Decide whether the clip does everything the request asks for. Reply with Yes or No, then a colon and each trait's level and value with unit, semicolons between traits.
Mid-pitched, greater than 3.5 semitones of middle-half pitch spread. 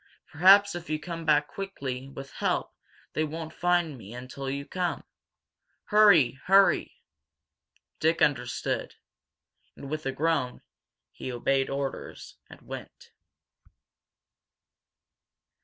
Yes: medium, 150 Hz; average, 4.4 semitones